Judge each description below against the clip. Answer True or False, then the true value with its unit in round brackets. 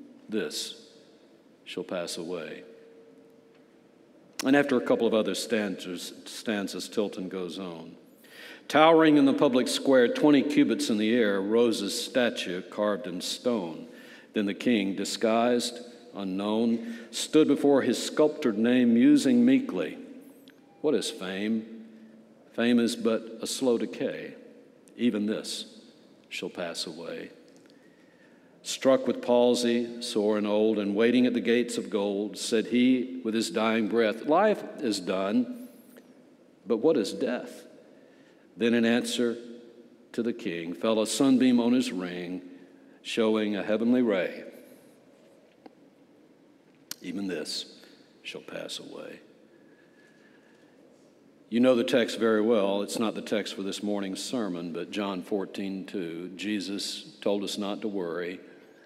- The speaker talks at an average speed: False (130 wpm)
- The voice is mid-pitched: False (115 Hz)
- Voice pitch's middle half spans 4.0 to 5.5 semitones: False (3.5 semitones)